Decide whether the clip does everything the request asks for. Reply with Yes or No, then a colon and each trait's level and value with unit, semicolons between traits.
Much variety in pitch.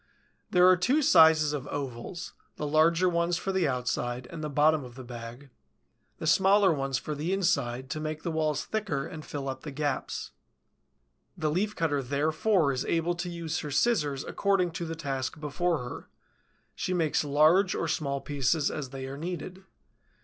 No: average, 4.0 semitones